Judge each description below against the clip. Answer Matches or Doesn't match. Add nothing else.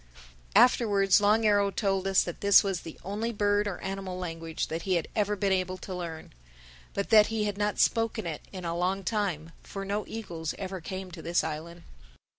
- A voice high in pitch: Matches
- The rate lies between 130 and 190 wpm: Doesn't match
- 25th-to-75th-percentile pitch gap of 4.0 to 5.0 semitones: Doesn't match